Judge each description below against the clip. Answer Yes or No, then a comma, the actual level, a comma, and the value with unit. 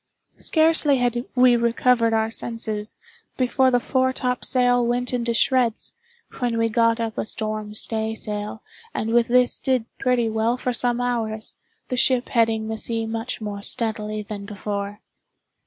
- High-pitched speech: Yes, high, 230 Hz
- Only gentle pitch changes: Yes, narrow, 2.1 semitones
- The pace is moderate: Yes, average, 150 wpm